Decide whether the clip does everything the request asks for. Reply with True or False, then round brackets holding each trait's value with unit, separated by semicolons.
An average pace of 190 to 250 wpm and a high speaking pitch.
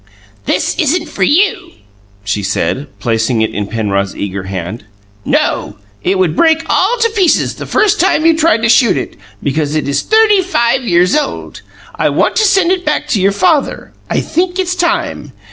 False (180 wpm; 260 Hz)